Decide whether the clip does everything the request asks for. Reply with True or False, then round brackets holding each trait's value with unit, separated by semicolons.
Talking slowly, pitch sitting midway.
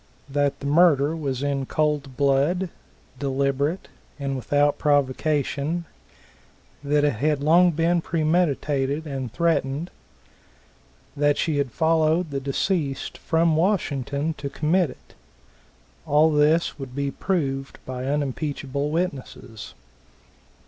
True (110 wpm; 145 Hz)